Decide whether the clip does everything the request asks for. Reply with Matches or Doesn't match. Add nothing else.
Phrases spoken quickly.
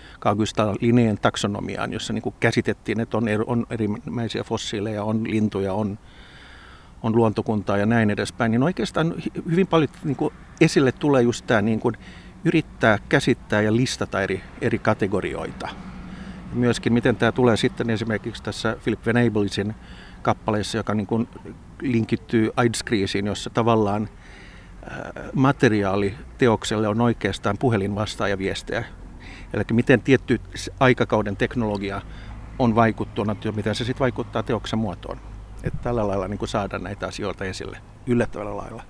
Doesn't match